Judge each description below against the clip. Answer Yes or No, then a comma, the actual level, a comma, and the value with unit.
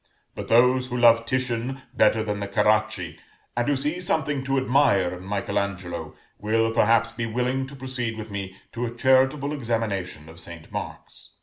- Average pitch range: Yes, average, 4.0 semitones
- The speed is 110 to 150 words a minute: No, average, 175 wpm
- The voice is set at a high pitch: No, low, 115 Hz